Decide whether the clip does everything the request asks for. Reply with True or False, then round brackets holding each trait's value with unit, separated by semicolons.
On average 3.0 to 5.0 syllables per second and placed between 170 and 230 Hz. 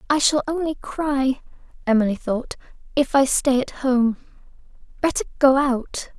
False (4.4 syllables/s; 265 Hz)